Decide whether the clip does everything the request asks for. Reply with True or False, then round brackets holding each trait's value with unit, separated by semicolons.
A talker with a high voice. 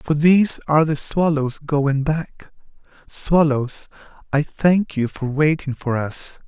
False (150 Hz)